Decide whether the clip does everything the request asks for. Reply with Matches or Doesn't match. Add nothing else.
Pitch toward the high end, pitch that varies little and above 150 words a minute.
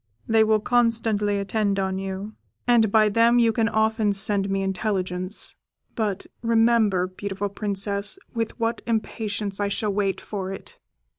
Doesn't match